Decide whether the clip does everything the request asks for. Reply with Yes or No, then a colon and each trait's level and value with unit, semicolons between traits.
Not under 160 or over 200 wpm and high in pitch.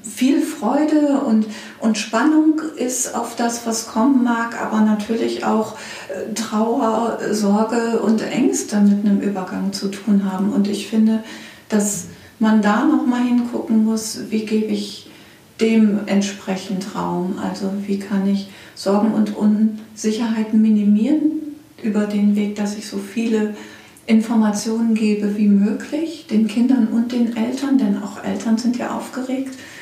No: average, 140 wpm; high, 220 Hz